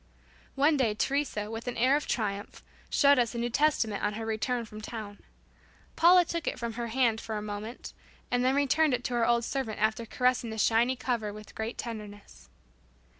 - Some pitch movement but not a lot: Yes, average, 3.0 semitones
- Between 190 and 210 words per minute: Yes, average, 195 wpm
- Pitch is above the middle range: Yes, high, 235 Hz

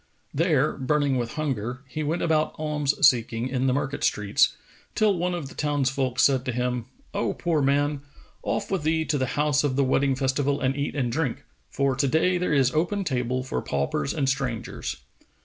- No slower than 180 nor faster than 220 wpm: Yes, average, 190 wpm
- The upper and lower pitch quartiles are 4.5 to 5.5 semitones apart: No, average, 2.9 semitones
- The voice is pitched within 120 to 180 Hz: Yes, medium, 140 Hz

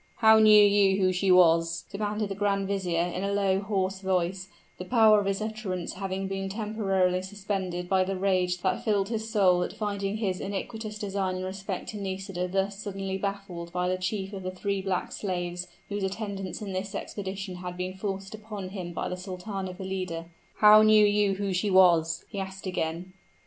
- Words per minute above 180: Yes, average, 190 wpm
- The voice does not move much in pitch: Yes, narrow, 1.7 semitones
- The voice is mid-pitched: No, high, 195 Hz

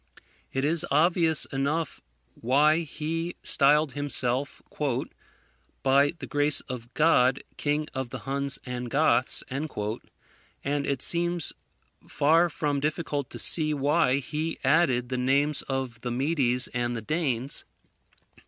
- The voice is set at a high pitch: No, medium, 140 Hz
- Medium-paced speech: No, slow, 125 wpm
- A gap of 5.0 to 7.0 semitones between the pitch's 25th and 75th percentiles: No, average, 3.2 semitones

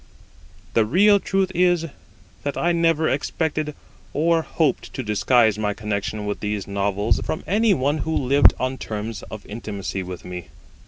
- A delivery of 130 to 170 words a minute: Yes, average, 155 wpm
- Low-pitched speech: Yes, low, 130 Hz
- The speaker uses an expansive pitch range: Yes, wide, 7.7 semitones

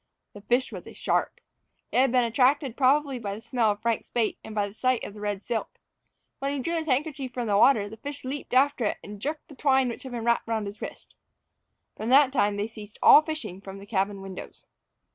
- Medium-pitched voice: No, high, 235 Hz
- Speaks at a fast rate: Yes, fast, 235 wpm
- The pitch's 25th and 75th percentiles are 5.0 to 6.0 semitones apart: No, average, 4.6 semitones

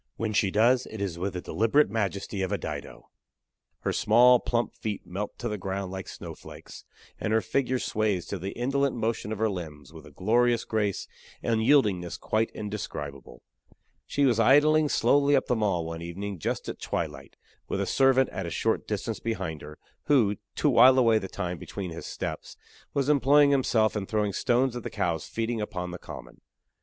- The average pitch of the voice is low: Yes, low, 110 Hz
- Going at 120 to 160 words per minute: No, average, 190 wpm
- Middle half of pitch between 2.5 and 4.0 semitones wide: No, average, 4.5 semitones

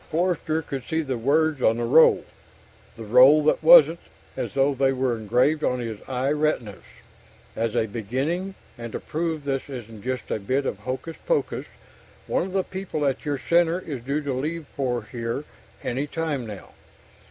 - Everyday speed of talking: Yes, average, 175 wpm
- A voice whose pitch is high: No, low, 135 Hz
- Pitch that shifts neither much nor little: Yes, average, 4.7 semitones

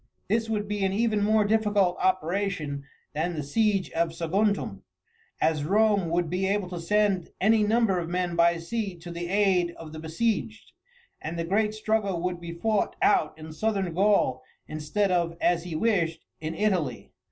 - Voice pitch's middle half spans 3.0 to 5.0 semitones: Yes, average, 3.9 semitones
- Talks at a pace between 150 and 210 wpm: Yes, average, 175 wpm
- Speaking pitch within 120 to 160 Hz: No, medium, 185 Hz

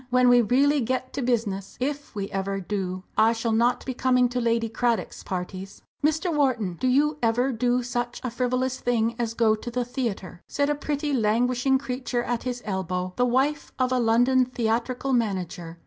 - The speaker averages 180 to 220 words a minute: Yes, average, 185 wpm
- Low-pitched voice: No, high, 245 Hz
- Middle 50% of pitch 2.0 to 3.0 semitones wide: Yes, average, 2.7 semitones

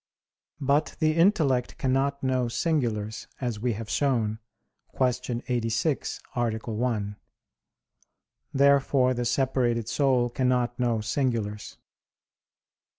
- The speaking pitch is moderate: No, low, 125 Hz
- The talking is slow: Yes, slow, 95 wpm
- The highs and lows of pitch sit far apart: No, average, 2.9 semitones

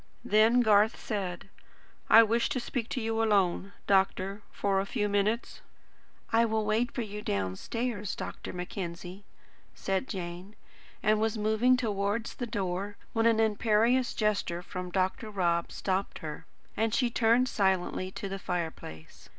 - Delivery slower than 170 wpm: Yes, average, 145 wpm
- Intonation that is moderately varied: Yes, average, 3.1 semitones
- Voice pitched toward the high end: Yes, high, 205 Hz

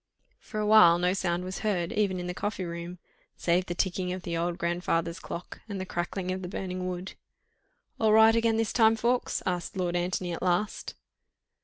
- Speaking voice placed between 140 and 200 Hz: Yes, medium, 185 Hz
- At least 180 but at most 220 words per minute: Yes, average, 195 wpm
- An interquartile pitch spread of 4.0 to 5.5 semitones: No, average, 2.9 semitones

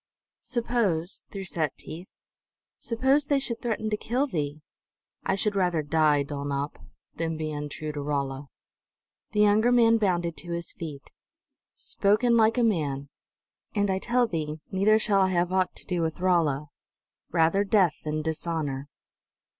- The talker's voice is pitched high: No, medium, 175 Hz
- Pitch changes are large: Yes, wide, 5.8 semitones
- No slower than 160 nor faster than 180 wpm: No, average, 150 wpm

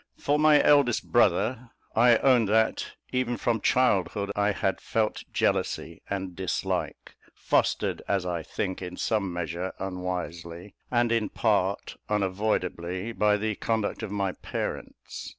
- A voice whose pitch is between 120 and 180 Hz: No, low, 105 Hz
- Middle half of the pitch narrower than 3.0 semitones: No, average, 3.8 semitones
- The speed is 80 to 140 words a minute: Yes, slow, 135 wpm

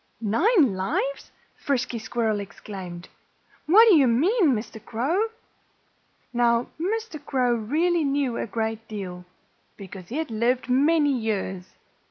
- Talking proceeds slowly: Yes, slow, 125 wpm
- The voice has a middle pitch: No, high, 245 Hz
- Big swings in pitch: Yes, wide, 6.5 semitones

